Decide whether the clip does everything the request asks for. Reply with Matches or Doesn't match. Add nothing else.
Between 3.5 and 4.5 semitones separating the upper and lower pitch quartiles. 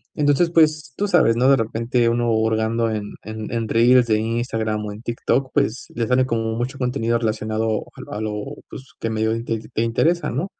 Doesn't match